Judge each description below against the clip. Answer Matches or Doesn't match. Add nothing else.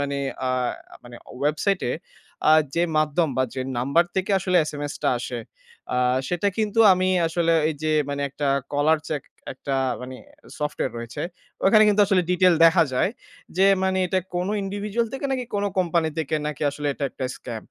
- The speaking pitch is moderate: Matches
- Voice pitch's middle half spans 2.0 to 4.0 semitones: Doesn't match